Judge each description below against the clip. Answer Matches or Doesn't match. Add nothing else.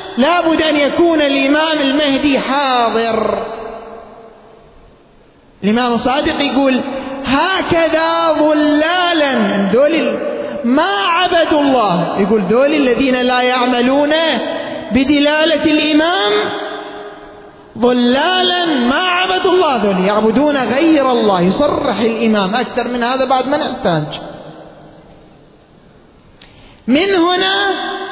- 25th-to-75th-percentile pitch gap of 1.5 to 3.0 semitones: Doesn't match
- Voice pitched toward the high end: Matches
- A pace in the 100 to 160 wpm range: Doesn't match